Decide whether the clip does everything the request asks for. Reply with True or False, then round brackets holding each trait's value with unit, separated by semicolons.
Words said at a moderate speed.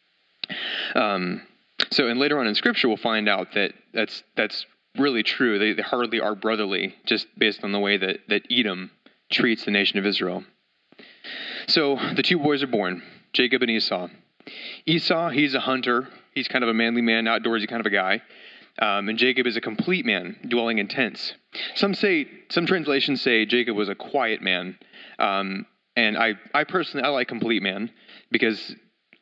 True (180 wpm)